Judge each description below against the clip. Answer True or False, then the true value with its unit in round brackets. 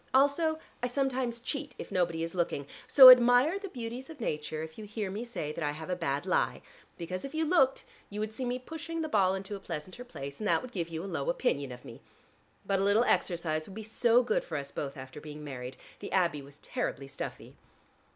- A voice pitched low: False (200 Hz)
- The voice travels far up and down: True (8.2 semitones)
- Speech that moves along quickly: True (230 wpm)